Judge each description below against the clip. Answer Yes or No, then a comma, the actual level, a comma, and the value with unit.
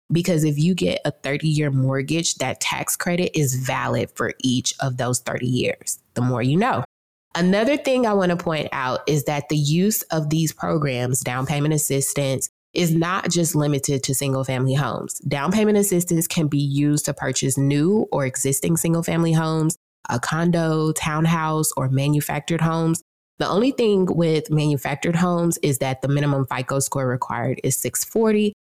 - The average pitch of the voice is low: No, medium, 150 Hz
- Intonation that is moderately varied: Yes, average, 3.7 semitones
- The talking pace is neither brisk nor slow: Yes, average, 170 wpm